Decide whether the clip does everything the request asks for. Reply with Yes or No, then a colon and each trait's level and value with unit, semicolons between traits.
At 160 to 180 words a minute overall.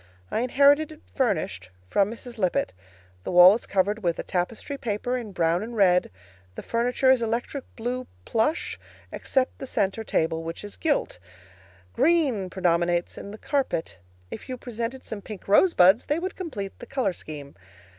Yes: average, 165 wpm